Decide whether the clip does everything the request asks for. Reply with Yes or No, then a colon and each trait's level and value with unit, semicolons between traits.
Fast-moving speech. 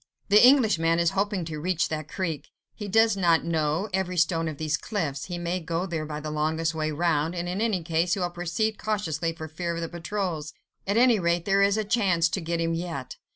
Yes: fast, 225 wpm